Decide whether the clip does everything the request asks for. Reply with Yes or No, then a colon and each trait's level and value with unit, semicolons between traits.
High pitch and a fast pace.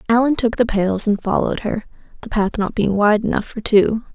Yes: high, 215 Hz; fast, 215 wpm